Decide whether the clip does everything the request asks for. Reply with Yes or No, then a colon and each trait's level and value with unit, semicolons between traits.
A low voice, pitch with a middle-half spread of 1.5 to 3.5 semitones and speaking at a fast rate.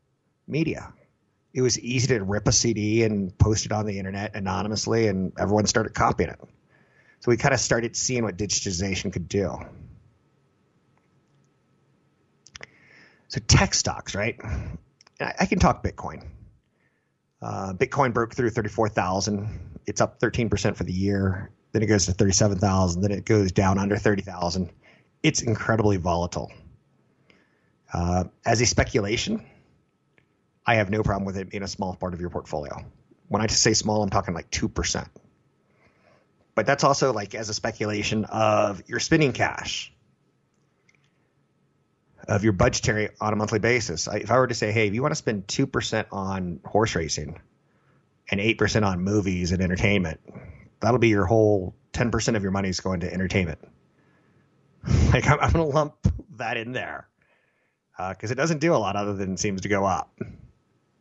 No: low, 105 Hz; average, 3.0 semitones; average, 165 wpm